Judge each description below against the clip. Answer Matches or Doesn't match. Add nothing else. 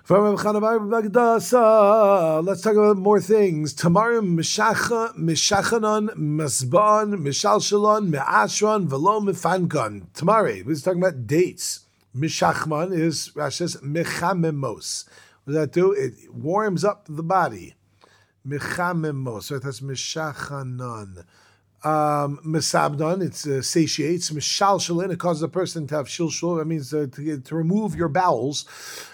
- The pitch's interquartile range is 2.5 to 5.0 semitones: Doesn't match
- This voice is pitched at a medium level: Matches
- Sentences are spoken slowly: Matches